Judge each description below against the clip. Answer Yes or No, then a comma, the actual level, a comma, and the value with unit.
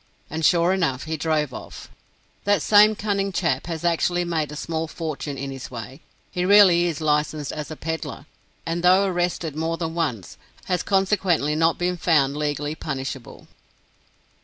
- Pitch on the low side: No, medium, 160 Hz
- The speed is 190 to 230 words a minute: No, average, 160 wpm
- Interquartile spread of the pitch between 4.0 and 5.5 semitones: No, average, 3.0 semitones